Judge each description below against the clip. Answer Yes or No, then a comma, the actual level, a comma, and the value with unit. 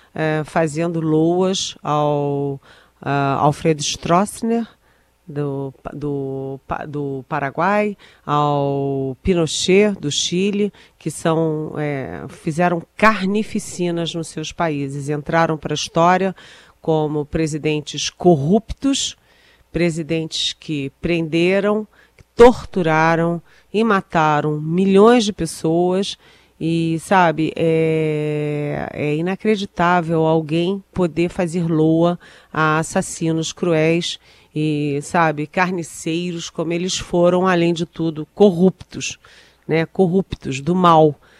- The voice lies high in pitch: No, medium, 165 Hz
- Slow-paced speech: Yes, slow, 95 wpm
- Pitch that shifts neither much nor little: Yes, average, 3.1 semitones